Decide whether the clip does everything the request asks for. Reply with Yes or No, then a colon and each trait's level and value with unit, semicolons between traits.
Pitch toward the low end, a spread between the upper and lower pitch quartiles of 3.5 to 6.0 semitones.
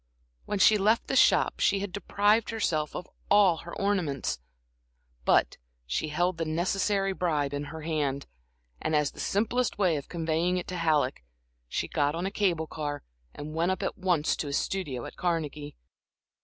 No: medium, 170 Hz; average, 4.5 semitones